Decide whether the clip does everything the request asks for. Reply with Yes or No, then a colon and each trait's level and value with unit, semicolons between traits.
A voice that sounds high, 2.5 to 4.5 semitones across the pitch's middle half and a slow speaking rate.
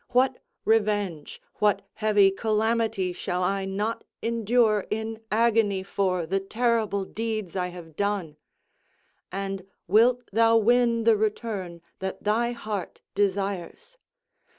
Yes: high, 210 Hz; average, 2.9 semitones; slow, 115 wpm